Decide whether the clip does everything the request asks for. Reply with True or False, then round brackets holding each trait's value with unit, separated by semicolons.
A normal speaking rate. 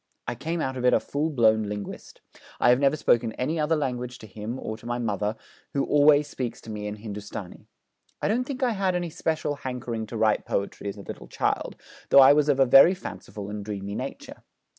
False (220 wpm)